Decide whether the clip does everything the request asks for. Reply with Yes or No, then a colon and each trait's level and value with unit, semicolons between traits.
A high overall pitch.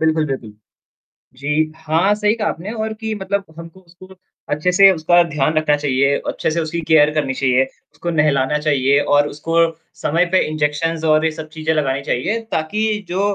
No: medium, 155 Hz